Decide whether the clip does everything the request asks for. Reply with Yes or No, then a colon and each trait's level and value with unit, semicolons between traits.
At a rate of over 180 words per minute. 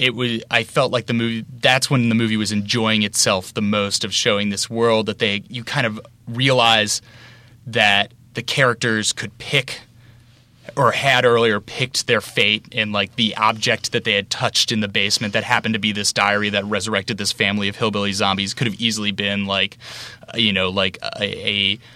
Yes: average, 195 wpm